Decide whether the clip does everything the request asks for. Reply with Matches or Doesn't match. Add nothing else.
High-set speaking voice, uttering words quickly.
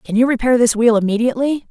Matches